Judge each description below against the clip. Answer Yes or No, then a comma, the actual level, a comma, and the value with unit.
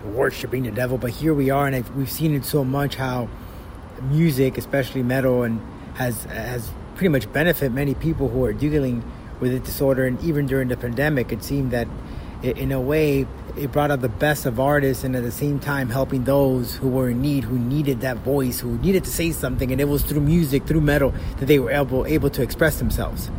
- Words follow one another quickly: Yes, fast, 220 wpm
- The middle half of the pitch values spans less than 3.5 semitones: Yes, narrow, 2.5 semitones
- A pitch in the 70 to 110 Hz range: No, low, 135 Hz